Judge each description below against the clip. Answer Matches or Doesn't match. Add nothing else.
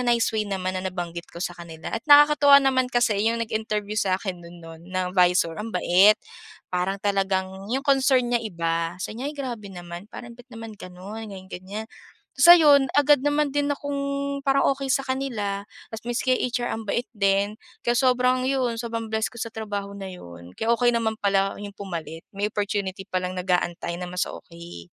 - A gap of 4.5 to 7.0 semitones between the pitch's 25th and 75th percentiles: Matches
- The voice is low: Doesn't match